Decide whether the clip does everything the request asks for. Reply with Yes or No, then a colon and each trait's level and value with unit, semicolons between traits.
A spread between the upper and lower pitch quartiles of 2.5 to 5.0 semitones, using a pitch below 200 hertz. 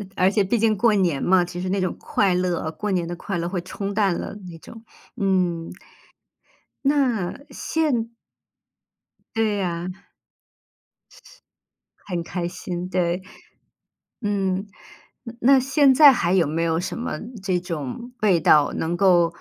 Yes: average, 3.5 semitones; medium, 185 Hz